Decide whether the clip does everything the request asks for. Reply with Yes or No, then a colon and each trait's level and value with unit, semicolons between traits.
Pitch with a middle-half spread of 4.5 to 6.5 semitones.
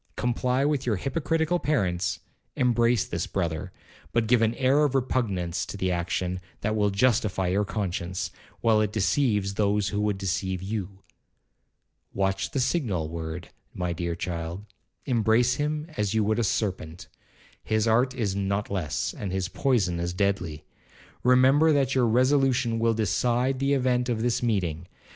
Yes: average, 5.1 semitones